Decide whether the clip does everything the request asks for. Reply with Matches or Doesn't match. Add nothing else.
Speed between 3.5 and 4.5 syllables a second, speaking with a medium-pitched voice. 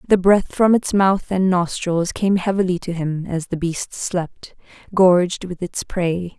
Matches